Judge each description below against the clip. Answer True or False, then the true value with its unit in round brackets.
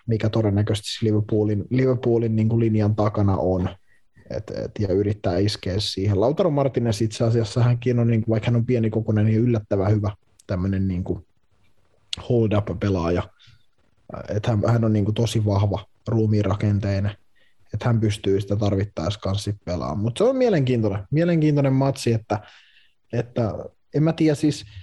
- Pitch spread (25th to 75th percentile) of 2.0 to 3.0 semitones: True (2.4 semitones)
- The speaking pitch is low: True (105 Hz)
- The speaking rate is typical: True (145 wpm)